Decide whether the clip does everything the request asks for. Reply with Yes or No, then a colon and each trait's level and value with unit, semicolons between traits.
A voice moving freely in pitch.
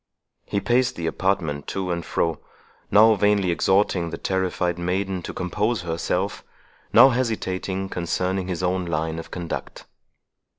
No: narrow, 2.5 semitones